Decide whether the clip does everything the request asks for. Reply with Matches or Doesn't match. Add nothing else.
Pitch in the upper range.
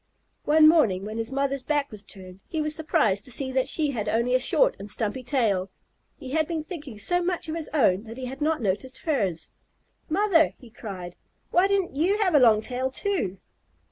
Matches